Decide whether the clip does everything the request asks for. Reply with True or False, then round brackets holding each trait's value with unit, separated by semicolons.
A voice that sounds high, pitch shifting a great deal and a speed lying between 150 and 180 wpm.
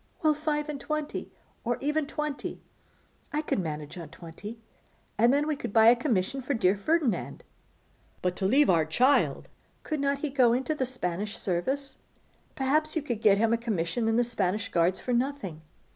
True (245 Hz; 6.4 semitones; 175 wpm)